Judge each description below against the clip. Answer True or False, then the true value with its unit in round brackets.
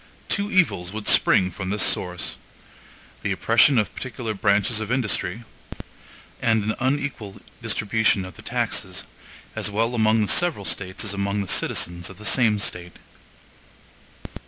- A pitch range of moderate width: True (3.2 semitones)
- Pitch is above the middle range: False (105 Hz)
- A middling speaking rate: True (145 wpm)